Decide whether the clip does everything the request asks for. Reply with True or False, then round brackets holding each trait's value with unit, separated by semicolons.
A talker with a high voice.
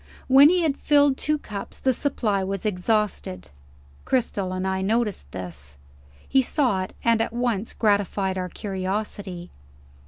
True (205 Hz)